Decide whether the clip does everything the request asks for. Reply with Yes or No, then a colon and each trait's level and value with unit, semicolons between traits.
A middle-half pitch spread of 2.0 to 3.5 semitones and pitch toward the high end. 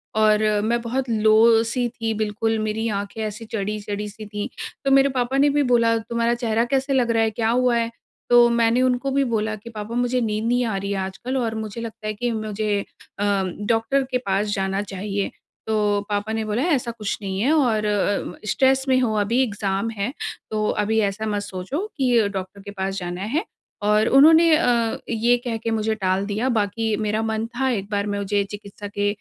Yes: average, 2.8 semitones; high, 220 Hz